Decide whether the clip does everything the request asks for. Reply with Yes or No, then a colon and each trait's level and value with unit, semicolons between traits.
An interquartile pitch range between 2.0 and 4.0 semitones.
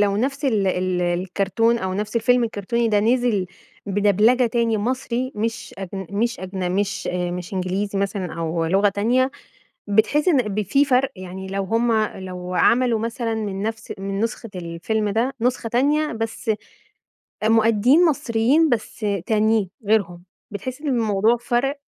Yes: average, 3.7 semitones